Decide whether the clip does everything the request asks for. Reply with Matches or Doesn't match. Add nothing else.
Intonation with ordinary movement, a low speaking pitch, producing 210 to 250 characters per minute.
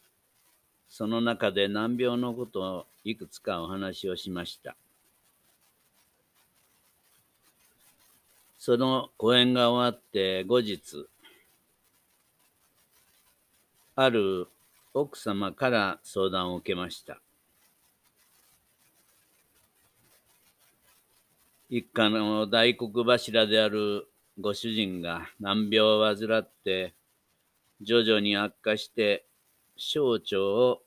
Doesn't match